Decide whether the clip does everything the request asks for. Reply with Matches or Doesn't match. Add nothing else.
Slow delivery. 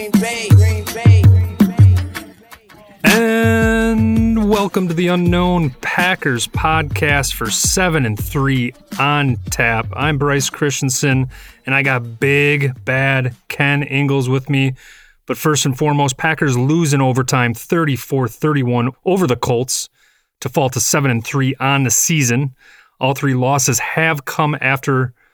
Matches